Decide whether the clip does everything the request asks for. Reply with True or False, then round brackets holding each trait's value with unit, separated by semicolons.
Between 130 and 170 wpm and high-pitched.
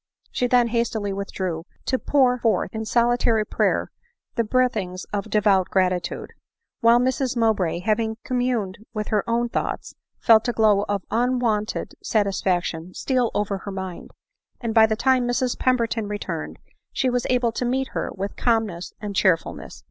True (155 wpm; 220 Hz)